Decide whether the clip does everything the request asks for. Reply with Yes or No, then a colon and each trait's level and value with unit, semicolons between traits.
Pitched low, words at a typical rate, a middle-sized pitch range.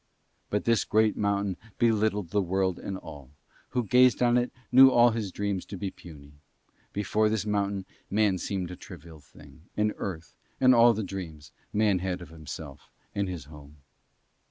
Yes: low, 100 Hz; average, 170 wpm; average, 3.5 semitones